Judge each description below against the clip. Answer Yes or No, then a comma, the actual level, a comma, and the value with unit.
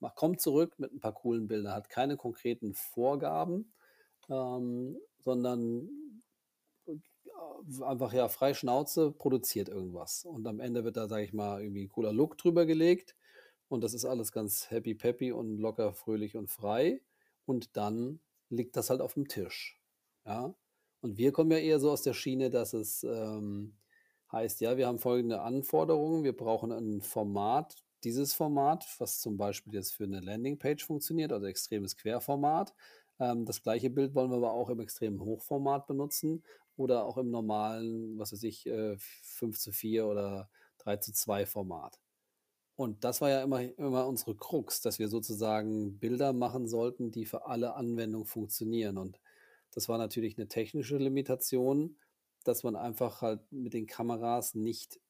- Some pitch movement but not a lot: Yes, average, 3.8 semitones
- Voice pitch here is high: No, low, 120 Hz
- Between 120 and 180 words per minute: Yes, average, 165 wpm